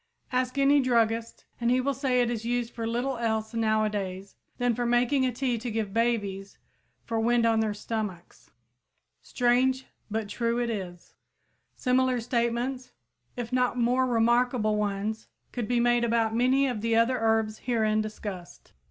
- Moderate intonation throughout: No, narrow, 2.2 semitones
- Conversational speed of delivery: Yes, average, 160 wpm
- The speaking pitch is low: No, high, 235 Hz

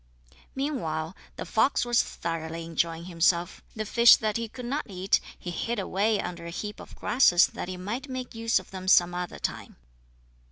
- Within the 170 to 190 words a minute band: Yes, average, 185 wpm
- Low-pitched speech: No, high, 190 Hz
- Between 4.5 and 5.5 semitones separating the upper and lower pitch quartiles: Yes, average, 5.2 semitones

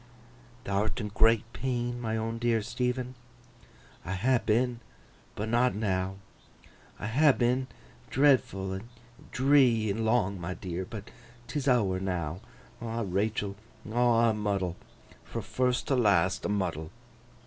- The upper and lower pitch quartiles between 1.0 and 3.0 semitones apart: No, average, 4.1 semitones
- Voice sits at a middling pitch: No, low, 110 Hz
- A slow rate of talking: Yes, slow, 125 wpm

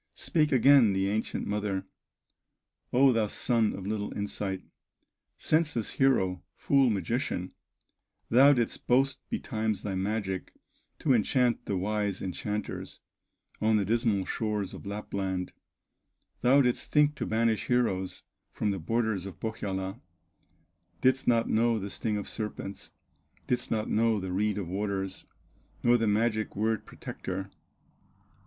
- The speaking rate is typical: No, slow, 130 wpm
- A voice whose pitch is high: No, low, 110 Hz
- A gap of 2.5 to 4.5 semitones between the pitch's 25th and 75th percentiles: Yes, average, 3.3 semitones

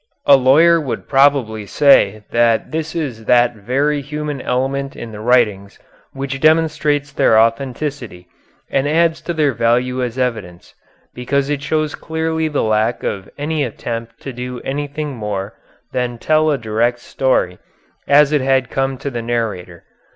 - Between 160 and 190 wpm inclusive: No, average, 150 wpm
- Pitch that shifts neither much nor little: Yes, average, 4.0 semitones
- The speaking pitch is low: Yes, low, 130 Hz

